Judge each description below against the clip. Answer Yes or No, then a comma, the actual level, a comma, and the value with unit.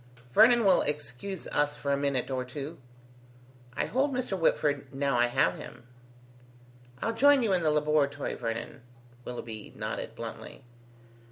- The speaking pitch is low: No, medium, 145 Hz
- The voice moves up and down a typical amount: No, wide, 6.5 semitones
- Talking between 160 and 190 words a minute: No, average, 150 wpm